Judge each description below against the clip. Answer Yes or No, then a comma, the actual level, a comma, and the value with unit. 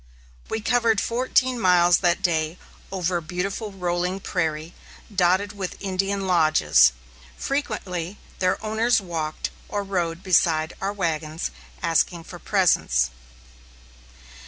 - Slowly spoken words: Yes, slow, 110 wpm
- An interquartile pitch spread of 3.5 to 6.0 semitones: No, average, 3.1 semitones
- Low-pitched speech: No, medium, 180 Hz